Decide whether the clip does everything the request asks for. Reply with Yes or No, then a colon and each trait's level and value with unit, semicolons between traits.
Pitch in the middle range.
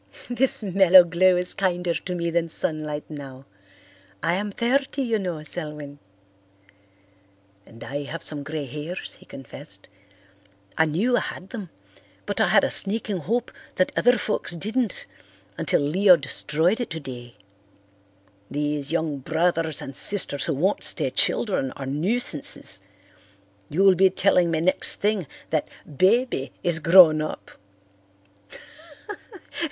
Yes: medium, 170 Hz